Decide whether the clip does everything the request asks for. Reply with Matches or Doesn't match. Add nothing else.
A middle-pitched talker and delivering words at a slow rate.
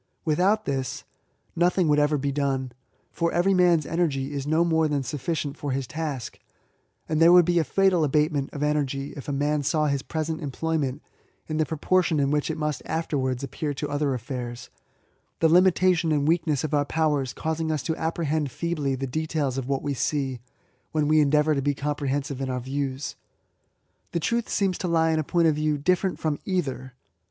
Doesn't match